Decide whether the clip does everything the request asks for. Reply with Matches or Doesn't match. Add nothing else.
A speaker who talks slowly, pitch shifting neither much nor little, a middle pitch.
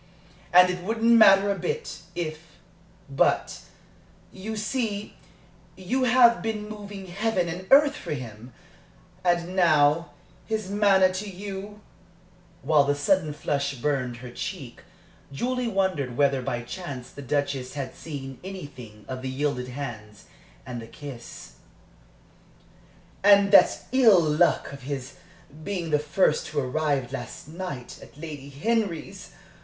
Doesn't match